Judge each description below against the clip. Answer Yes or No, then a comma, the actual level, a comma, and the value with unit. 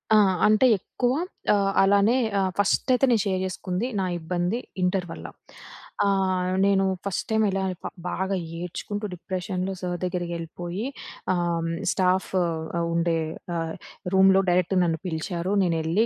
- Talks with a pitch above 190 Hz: No, medium, 185 Hz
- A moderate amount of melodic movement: No, narrow, 2.0 semitones